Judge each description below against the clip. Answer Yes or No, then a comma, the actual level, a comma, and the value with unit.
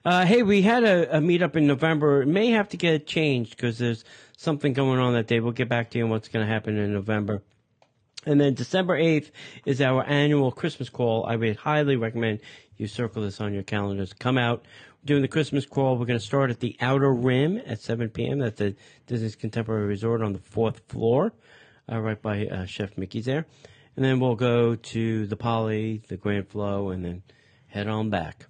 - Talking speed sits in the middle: No, fast, 215 wpm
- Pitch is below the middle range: Yes, low, 120 Hz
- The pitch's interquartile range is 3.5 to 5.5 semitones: Yes, average, 4.4 semitones